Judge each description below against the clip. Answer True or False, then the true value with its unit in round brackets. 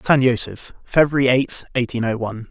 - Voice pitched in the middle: False (125 Hz)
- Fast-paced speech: False (170 wpm)